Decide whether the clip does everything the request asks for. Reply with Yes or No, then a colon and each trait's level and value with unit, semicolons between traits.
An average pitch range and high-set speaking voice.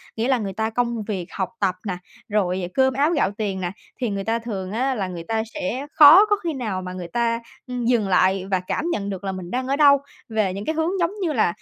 No: wide, 5.7 semitones; high, 220 Hz